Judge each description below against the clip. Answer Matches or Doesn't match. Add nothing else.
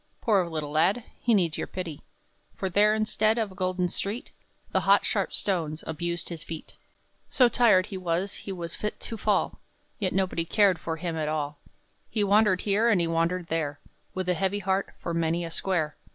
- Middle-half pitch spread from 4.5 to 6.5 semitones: Doesn't match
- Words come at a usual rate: Matches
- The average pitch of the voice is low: Doesn't match